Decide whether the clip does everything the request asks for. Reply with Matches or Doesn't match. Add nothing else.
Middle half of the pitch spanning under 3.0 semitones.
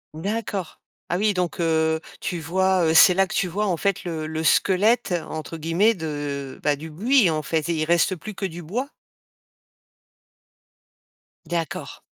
Doesn't match